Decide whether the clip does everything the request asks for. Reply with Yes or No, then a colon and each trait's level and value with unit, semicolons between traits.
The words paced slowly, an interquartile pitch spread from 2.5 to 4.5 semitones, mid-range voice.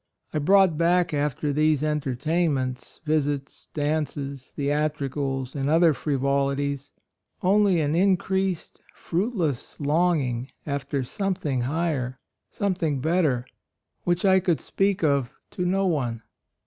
Yes: slow, 110 wpm; average, 4.1 semitones; medium, 150 Hz